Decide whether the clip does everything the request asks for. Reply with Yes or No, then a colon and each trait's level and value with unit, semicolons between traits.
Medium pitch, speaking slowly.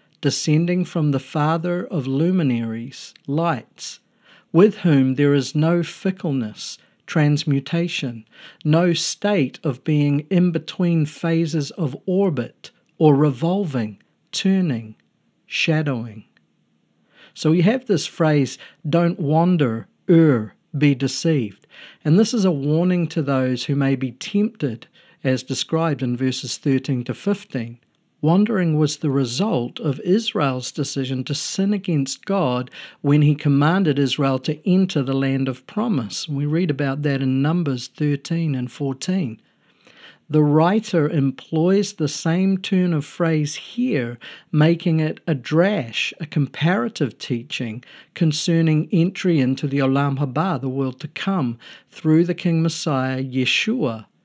Yes: medium, 155 Hz; slow, 130 wpm